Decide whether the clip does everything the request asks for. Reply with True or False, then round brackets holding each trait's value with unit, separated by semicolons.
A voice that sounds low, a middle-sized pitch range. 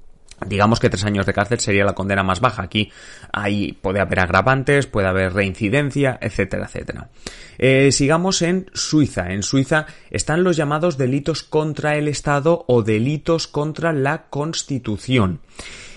False (130 Hz; 6.9 semitones)